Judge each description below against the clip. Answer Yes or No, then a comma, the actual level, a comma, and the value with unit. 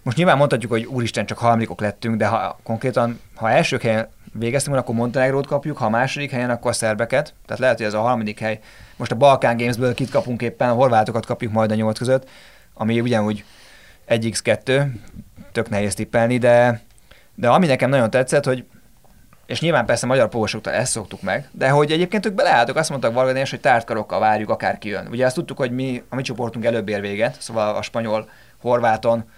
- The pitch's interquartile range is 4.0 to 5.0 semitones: No, average, 2.9 semitones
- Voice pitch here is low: Yes, low, 120 Hz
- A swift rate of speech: Yes, fast, 190 wpm